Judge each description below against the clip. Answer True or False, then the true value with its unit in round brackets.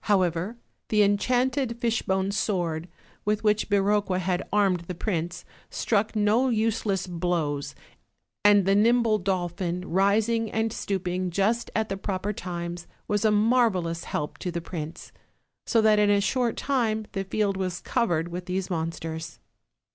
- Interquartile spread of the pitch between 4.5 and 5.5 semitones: False (3.5 semitones)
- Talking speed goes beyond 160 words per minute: False (145 wpm)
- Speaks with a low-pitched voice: False (195 Hz)